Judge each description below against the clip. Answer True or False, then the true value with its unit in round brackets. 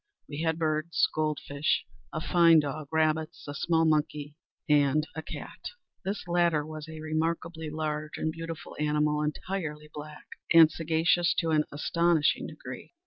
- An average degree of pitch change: False (1.5 semitones)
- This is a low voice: False (155 Hz)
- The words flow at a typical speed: True (145 wpm)